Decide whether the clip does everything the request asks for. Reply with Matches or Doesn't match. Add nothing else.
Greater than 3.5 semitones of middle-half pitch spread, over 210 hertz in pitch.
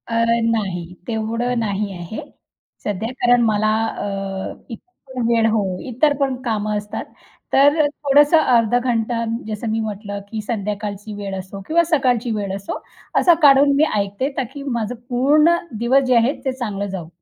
Matches